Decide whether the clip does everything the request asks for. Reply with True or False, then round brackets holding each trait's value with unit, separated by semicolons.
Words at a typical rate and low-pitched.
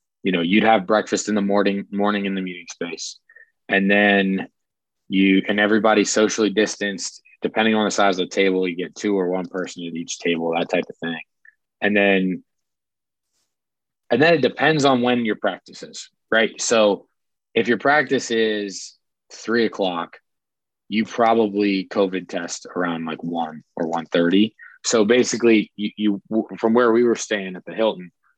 True (170 wpm; 100 Hz)